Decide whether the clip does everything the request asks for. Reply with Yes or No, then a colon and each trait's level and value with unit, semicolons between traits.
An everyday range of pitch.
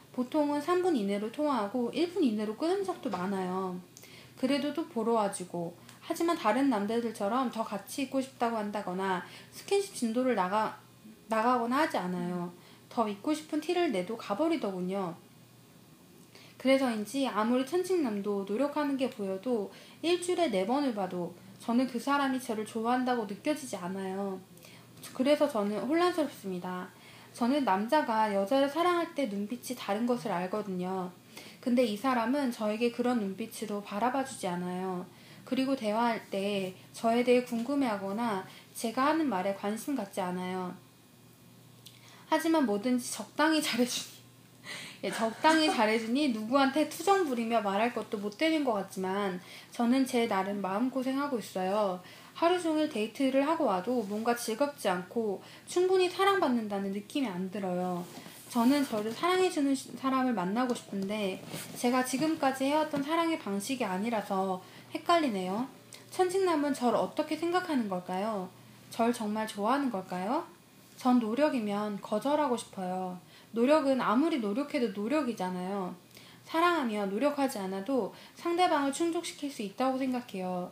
No: wide, 6.1 semitones